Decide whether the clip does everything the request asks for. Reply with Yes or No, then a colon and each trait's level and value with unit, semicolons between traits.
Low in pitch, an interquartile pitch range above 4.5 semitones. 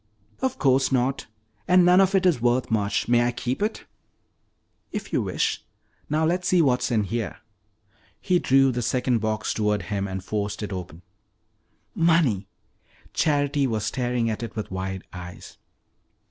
Yes: low, 120 Hz; wide, 5.6 semitones